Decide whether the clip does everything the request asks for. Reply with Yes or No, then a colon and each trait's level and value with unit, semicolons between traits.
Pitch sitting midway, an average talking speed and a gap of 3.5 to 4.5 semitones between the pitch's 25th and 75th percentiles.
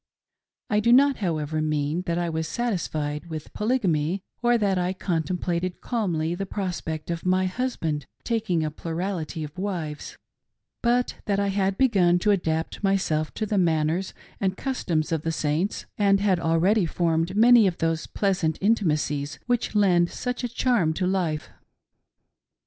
Yes: medium, 180 Hz; average, 155 wpm; average, 4.1 semitones